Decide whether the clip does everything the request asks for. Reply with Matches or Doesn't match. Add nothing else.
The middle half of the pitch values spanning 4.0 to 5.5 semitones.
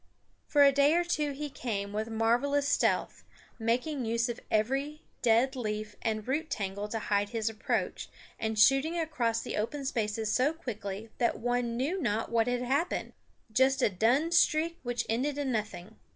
Matches